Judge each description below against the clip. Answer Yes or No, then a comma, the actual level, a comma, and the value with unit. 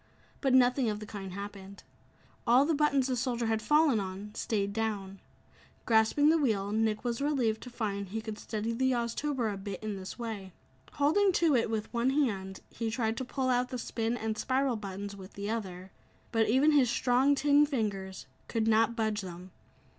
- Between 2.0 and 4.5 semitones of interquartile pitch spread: Yes, average, 4.2 semitones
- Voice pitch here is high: Yes, high, 225 Hz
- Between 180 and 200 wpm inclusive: Yes, average, 190 wpm